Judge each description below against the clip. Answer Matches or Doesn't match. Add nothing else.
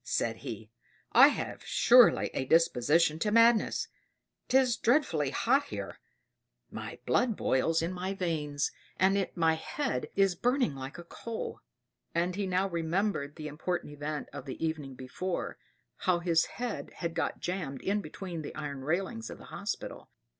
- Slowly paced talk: Doesn't match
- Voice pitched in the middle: Matches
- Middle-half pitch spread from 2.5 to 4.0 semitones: Doesn't match